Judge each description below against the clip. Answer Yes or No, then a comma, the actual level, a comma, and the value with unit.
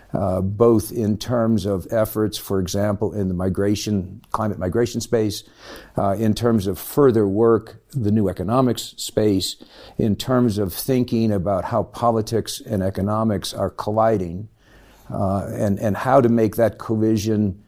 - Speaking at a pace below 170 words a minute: Yes, average, 145 wpm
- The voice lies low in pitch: Yes, low, 110 Hz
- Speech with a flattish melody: Yes, narrow, 2.2 semitones